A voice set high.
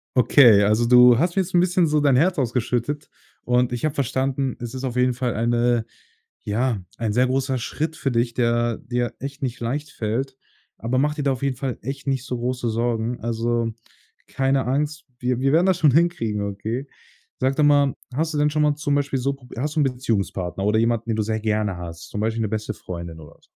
No: low, 125 Hz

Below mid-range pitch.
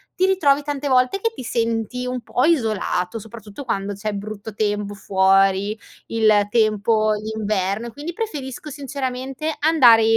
No: high, 230 Hz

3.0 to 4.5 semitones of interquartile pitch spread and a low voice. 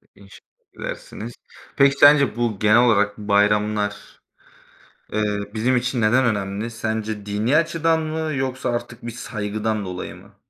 Yes: average, 3.6 semitones; low, 110 Hz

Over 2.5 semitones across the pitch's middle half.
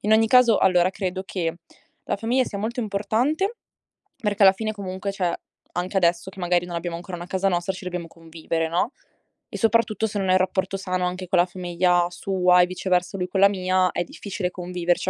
No: narrow, 2.1 semitones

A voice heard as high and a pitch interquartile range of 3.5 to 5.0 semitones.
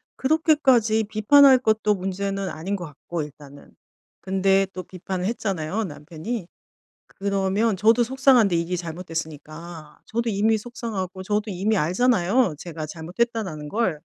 Yes: high, 195 Hz; average, 4.7 semitones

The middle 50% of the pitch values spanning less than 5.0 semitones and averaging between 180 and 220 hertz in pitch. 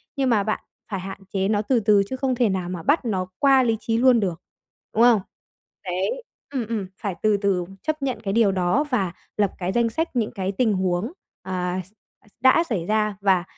Yes: average, 4.4 semitones; high, 210 Hz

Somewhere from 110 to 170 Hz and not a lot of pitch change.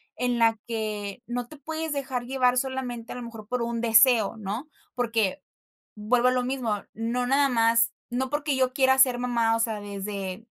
No: high, 240 Hz; narrow, 2.3 semitones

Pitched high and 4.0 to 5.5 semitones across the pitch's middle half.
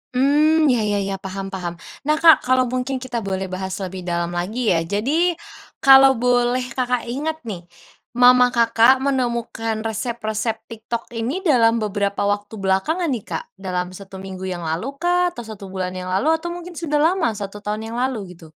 Yes: high, 230 Hz; average, 5.1 semitones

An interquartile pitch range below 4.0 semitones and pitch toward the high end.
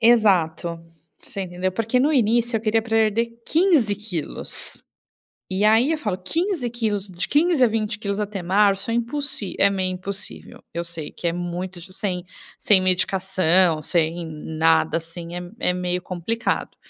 No: average, 4.3 semitones; high, 195 Hz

